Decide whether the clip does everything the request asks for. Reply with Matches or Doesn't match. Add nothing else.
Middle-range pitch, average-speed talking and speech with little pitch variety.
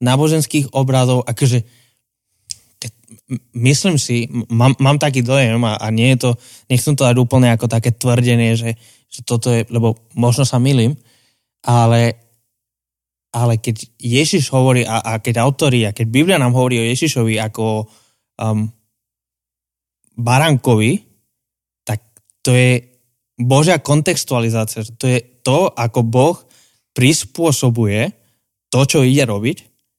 Doesn't match